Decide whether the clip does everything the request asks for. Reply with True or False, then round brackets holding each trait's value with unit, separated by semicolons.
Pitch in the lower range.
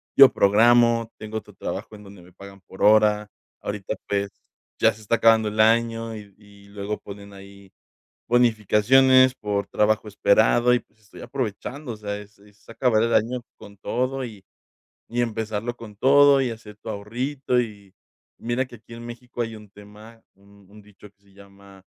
True (110 Hz)